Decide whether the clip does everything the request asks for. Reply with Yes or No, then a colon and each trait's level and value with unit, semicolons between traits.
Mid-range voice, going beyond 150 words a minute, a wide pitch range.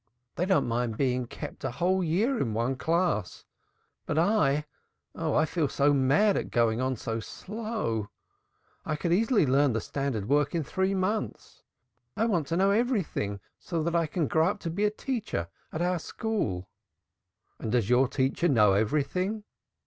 Yes: medium, 155 Hz; average, 170 wpm; wide, 7.2 semitones